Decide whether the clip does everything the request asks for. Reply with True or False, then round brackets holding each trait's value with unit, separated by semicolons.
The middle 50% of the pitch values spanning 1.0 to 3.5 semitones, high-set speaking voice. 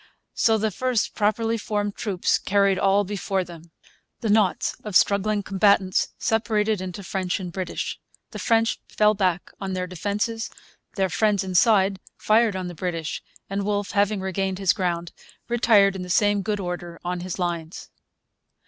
True (2.4 semitones; 195 Hz)